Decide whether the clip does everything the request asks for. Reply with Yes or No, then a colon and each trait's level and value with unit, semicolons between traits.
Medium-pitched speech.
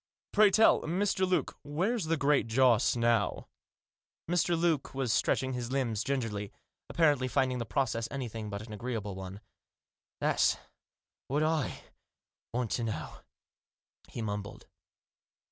No: low, 125 Hz